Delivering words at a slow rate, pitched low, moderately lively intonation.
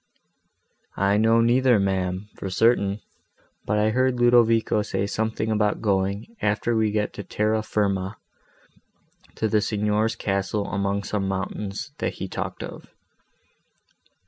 No: slow, 130 wpm; low, 105 Hz; narrow, 2.0 semitones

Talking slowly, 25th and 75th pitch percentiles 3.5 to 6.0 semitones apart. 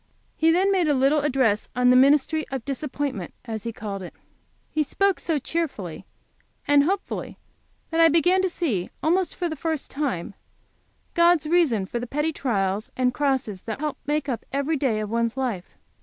No: average, 185 wpm; wide, 5.6 semitones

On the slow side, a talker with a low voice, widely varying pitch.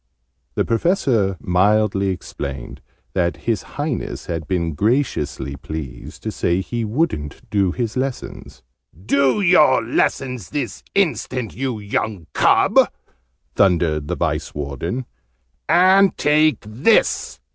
Yes: slow, 115 wpm; low, 110 Hz; wide, 7.7 semitones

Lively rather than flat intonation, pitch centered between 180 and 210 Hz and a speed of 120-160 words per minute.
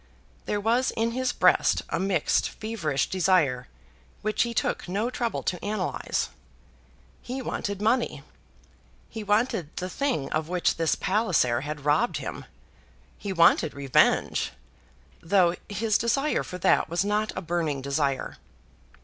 Yes: wide, 6.1 semitones; high, 190 Hz; slow, 135 wpm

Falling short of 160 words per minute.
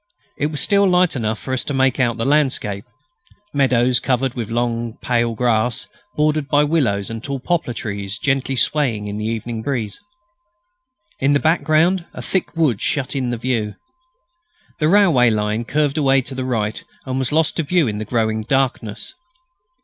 No: average, 175 wpm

